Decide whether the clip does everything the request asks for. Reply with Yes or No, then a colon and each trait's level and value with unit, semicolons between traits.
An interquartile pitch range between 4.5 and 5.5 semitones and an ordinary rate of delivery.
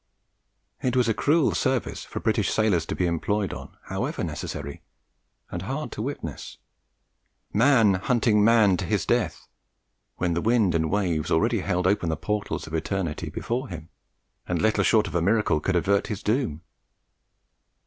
Yes: average, 4.9 semitones; average, 160 wpm